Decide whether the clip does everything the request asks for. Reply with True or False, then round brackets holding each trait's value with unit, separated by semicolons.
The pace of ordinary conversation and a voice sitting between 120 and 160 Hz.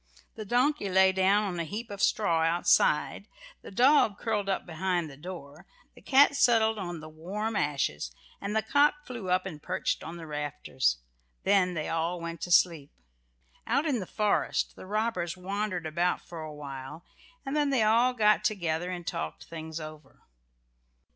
False (175 wpm; 185 Hz)